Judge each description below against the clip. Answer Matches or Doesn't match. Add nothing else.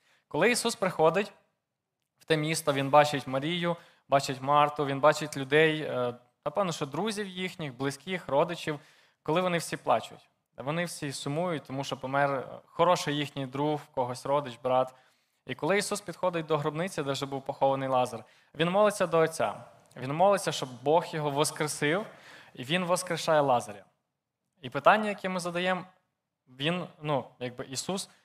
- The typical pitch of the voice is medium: Matches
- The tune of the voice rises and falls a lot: Doesn't match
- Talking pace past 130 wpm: Matches